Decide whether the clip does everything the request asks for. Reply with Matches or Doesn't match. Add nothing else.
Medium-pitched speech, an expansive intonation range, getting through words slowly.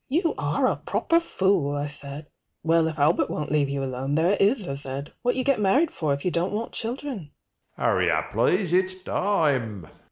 Doesn't match